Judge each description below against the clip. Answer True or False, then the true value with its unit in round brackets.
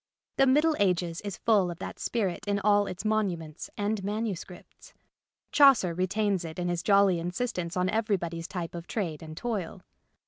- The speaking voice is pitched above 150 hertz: True (190 Hz)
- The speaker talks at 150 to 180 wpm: True (165 wpm)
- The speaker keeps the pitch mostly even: False (3.6 semitones)